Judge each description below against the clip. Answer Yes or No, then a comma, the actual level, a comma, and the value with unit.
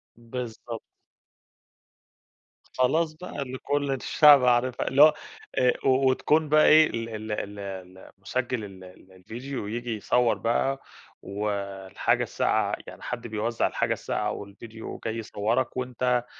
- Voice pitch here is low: Yes, low, 120 Hz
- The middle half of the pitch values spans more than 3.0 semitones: Yes, average, 3.5 semitones